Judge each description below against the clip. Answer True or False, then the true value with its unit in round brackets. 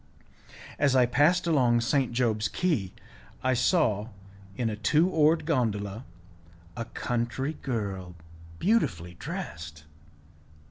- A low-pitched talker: True (120 Hz)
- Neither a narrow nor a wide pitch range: False (6.0 semitones)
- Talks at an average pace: False (105 wpm)